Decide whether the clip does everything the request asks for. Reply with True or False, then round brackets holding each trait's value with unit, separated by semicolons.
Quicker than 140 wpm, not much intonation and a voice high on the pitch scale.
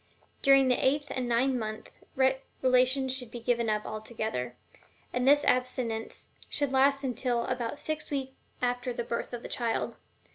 True (160 wpm; 2.3 semitones; 250 Hz)